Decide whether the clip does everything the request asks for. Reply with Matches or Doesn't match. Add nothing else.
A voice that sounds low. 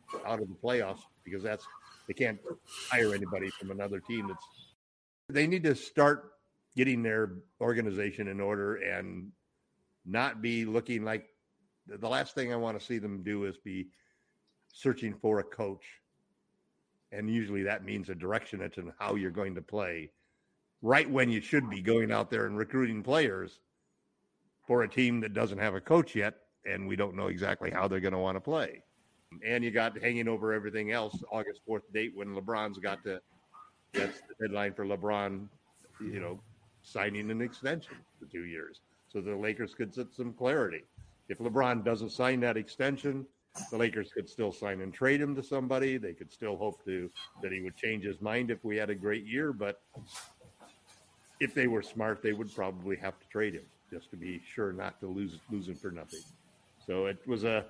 Matches